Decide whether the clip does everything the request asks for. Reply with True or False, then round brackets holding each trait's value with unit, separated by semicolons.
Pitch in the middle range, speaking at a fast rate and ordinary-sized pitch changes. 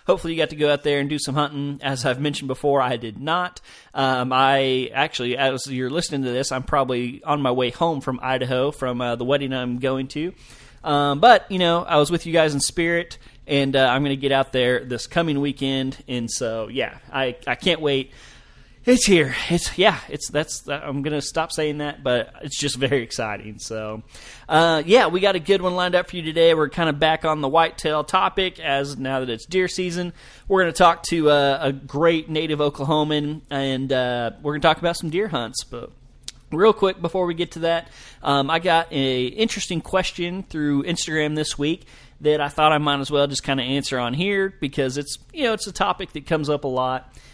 True (145 Hz; 230 wpm; 3.9 semitones)